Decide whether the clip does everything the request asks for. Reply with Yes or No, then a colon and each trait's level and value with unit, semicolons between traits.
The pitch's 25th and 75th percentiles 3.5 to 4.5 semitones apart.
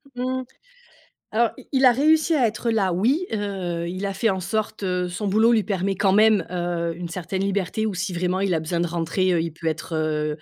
Yes: average, 4.0 semitones